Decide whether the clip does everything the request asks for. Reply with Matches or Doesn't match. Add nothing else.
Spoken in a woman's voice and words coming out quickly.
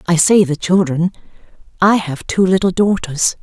Doesn't match